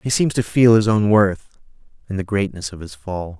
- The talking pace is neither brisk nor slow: No, fast, 230 wpm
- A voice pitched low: Yes, low, 100 Hz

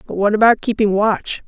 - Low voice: No, high, 210 Hz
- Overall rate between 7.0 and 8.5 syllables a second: No, 5.3 syllables/s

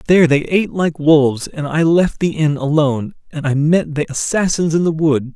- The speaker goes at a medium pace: No, fast, 215 wpm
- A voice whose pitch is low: No, medium, 155 Hz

